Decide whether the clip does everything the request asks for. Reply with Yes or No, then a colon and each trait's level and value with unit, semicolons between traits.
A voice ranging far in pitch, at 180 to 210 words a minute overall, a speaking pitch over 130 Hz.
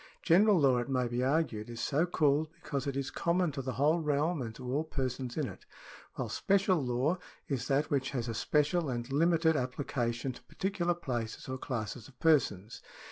No: average, 4.5 semitones; average, 190 wpm; medium, 140 Hz